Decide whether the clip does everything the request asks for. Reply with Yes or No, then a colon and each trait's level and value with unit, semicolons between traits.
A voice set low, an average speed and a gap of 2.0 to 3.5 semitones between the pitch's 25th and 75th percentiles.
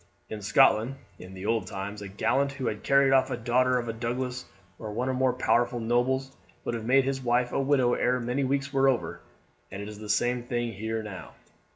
No: low, 120 Hz; fast, 220 wpm; average, 3.0 semitones